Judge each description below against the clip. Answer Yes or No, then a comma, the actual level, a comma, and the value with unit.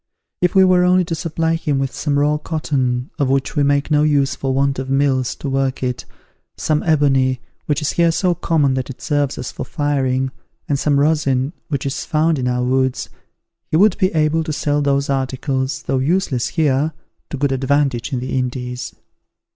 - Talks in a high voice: No, medium, 140 Hz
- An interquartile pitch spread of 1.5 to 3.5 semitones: Yes, average, 2.7 semitones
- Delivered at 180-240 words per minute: Yes, average, 195 wpm